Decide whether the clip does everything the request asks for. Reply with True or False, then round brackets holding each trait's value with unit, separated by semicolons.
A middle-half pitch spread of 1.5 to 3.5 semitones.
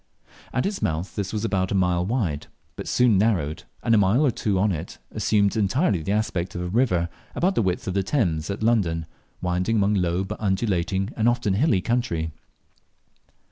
False (4.1 semitones)